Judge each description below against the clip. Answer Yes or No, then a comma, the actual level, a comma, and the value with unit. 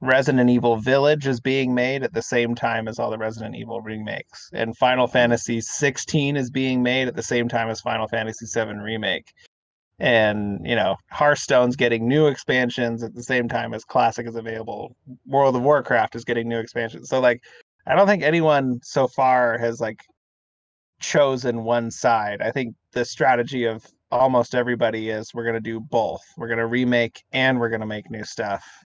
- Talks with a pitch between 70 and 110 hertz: No, low, 120 Hz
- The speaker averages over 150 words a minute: Yes, average, 190 wpm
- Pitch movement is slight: Yes, narrow, 2.2 semitones